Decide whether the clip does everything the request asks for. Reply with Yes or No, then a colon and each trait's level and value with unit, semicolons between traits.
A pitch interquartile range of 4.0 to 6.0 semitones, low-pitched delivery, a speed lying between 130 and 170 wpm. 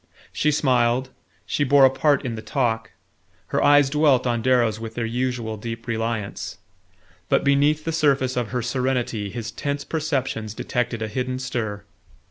No: average, 3.4 semitones; low, 125 Hz; average, 160 wpm